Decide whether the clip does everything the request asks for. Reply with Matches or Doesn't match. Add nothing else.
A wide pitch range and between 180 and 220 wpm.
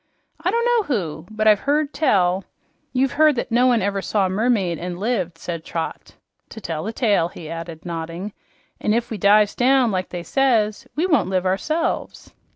Matches